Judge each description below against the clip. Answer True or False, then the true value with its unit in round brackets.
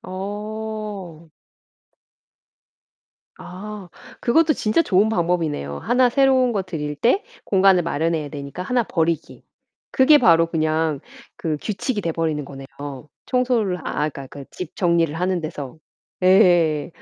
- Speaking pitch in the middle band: True (180 Hz)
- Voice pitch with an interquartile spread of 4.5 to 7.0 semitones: True (5.2 semitones)